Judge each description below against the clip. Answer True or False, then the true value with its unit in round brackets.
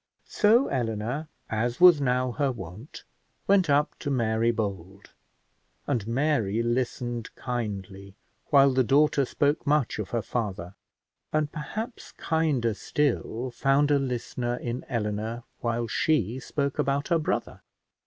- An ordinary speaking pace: False (130 wpm)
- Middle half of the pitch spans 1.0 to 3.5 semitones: False (4.3 semitones)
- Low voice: True (125 Hz)